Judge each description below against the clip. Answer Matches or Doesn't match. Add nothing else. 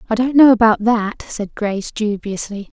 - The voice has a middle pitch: Doesn't match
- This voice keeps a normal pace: Matches